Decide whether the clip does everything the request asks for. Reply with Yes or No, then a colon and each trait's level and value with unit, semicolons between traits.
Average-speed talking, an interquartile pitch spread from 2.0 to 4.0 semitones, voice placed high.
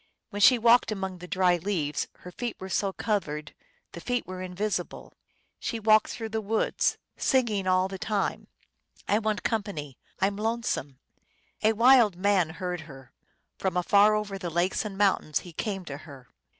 Yes: average, 170 wpm; average, 3.4 semitones; high, 195 Hz